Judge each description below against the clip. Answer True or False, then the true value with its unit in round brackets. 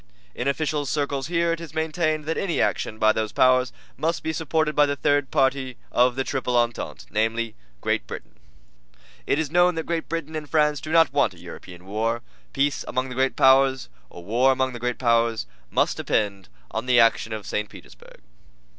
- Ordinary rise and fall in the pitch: True (4.9 semitones)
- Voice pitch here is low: True (130 Hz)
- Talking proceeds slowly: False (170 wpm)